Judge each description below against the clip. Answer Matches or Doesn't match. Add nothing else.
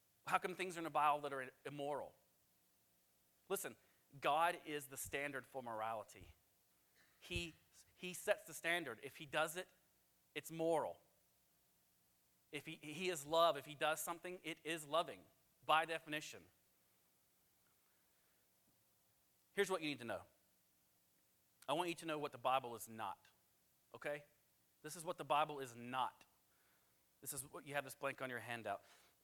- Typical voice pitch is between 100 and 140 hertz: Matches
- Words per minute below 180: Matches